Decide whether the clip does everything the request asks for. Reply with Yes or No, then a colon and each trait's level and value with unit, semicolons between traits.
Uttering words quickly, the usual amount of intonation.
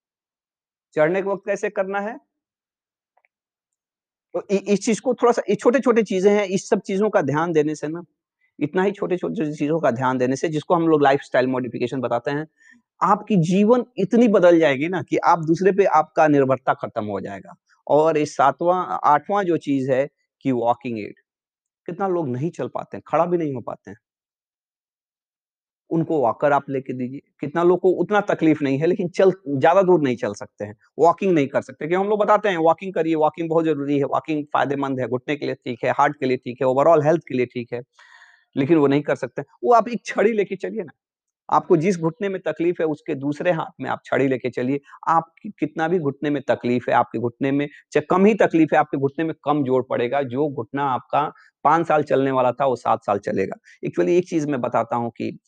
No: fast, 215 wpm; wide, 5.7 semitones